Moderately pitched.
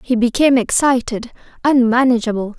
No: high, 240 Hz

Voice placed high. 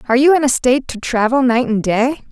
Yes: very high, 250 Hz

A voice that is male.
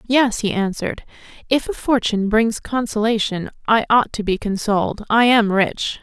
No: female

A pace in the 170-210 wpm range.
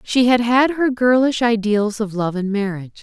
Yes: average, 200 wpm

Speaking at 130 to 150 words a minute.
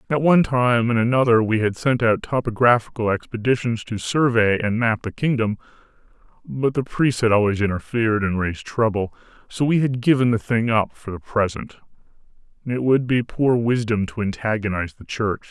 No: average, 175 wpm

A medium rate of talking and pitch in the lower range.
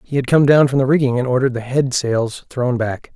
No: fast, 265 wpm; low, 130 Hz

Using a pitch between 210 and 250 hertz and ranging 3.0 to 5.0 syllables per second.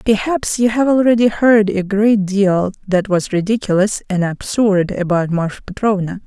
No: high, 200 Hz; 4.5 syllables/s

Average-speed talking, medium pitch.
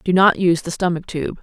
No: fast, 255 wpm; medium, 175 Hz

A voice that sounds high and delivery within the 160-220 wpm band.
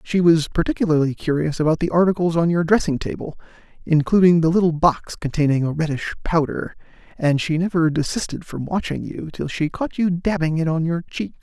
No: medium, 165 Hz; average, 185 wpm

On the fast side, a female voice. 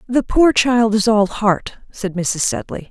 No: average, 185 wpm; female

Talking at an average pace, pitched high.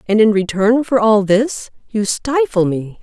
Yes: average, 180 wpm; high, 215 Hz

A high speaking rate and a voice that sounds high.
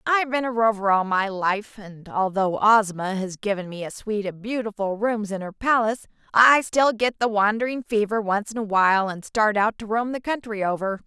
Yes: fast, 210 wpm; high, 215 Hz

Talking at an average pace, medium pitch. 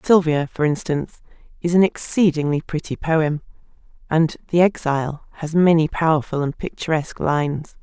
No: slow, 130 wpm; medium, 160 Hz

